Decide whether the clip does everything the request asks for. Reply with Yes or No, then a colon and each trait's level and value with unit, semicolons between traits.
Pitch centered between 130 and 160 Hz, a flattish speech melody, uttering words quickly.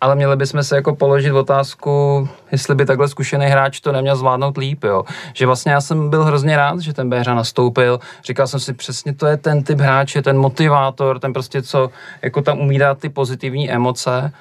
Yes: medium, 140 Hz; narrow, 1.4 semitones; fast, 205 wpm